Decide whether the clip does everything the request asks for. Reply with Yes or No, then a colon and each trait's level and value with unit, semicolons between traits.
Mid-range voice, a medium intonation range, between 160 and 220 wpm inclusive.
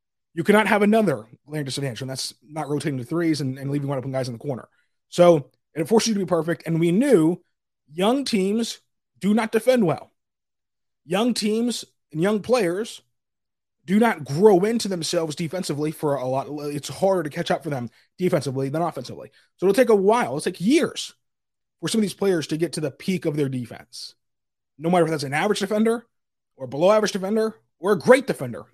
No: medium, 170 Hz; wide, 6.6 semitones; fast, 205 wpm